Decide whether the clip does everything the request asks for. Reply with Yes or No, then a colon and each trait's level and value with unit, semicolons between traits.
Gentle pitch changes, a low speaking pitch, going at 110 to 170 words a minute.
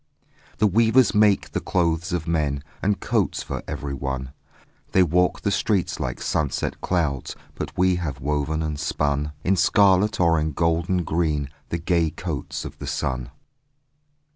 No: average, 4.0 semitones; very low, 80 Hz; average, 150 wpm